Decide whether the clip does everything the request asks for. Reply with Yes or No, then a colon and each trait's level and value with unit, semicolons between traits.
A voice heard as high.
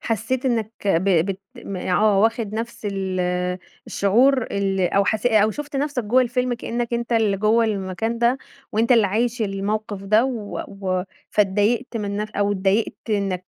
Yes: high, 215 Hz